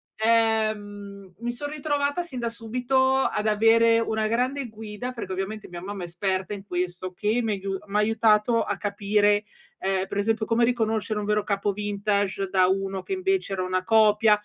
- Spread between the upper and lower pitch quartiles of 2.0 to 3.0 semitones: Yes, narrow, 2.6 semitones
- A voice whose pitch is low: No, high, 210 Hz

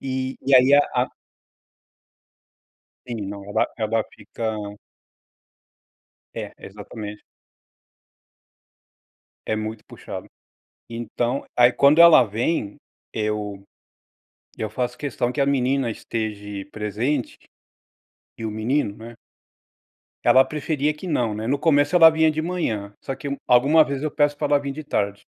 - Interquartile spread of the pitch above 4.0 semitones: Yes, average, 4.9 semitones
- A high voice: No, low, 125 Hz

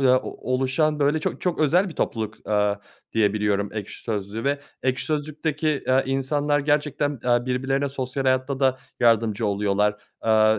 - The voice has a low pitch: Yes, low, 130 Hz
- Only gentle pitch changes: No, average, 4.8 semitones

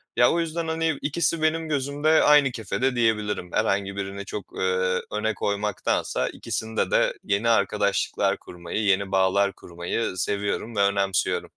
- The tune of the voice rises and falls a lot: Yes, wide, 5.7 semitones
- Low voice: Yes, low, 105 Hz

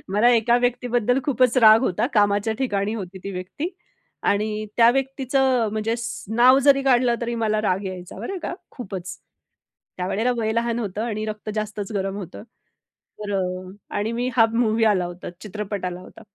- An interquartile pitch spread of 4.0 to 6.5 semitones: No, average, 3.1 semitones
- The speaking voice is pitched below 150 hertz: No, high, 220 Hz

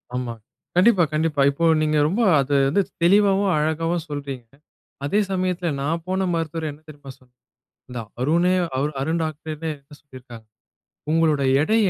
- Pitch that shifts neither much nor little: Yes, average, 3.6 semitones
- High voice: No, medium, 155 Hz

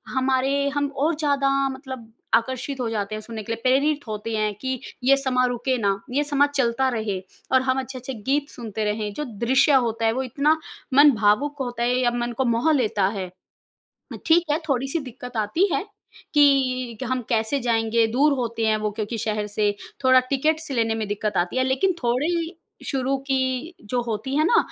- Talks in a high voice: Yes, very high, 255 Hz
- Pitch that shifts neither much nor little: Yes, average, 3.6 semitones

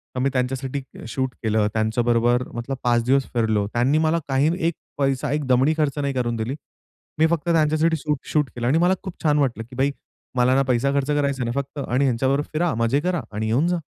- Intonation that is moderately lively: Yes, average, 3.6 semitones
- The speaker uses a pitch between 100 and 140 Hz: Yes, low, 135 Hz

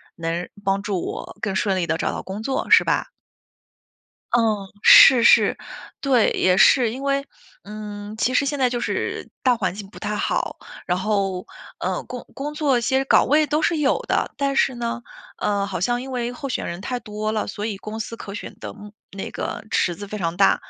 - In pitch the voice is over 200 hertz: Yes, high, 215 Hz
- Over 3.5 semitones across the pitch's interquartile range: Yes, average, 4.5 semitones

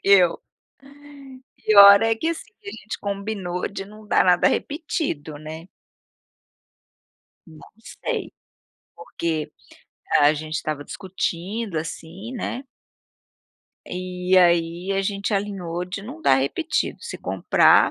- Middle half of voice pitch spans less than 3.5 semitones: No, average, 3.9 semitones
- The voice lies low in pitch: No, medium, 185 Hz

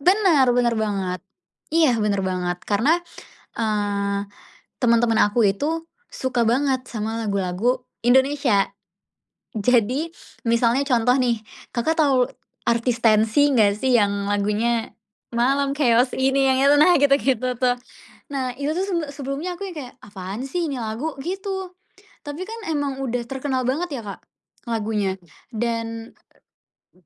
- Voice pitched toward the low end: No, high, 245 Hz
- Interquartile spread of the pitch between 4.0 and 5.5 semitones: Yes, average, 4.5 semitones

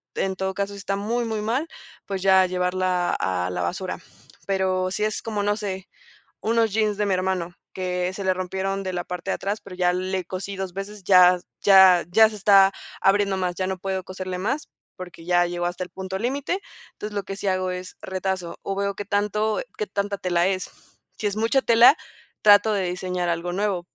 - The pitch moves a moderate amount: No, narrow, 2.0 semitones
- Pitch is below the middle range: No, high, 190 Hz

